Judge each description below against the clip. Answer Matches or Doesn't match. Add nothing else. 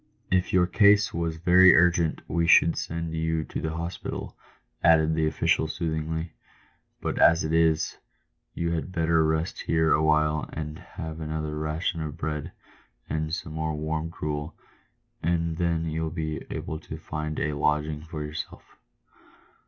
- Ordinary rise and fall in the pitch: Doesn't match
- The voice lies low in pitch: Matches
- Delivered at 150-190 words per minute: Matches